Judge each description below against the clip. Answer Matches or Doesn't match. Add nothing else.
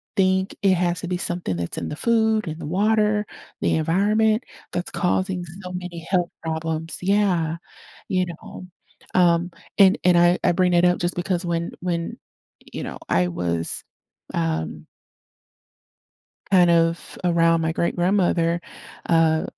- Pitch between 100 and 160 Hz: Doesn't match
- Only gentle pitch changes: Matches